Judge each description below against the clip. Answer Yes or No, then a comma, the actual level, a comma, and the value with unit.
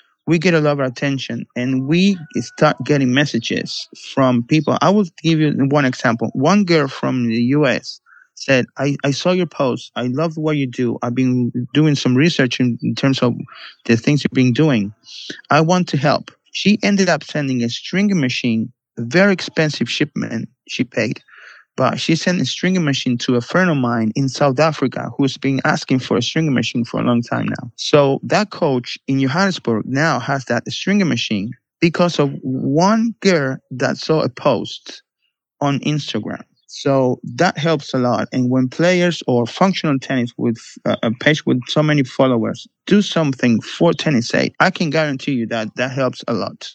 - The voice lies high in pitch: No, medium, 140 Hz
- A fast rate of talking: No, average, 185 wpm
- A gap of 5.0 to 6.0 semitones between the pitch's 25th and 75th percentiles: No, average, 4.4 semitones